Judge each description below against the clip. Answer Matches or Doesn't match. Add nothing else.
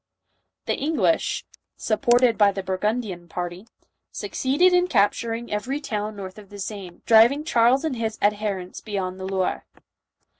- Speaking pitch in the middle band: Doesn't match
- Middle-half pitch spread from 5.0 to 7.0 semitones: Doesn't match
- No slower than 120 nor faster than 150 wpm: Matches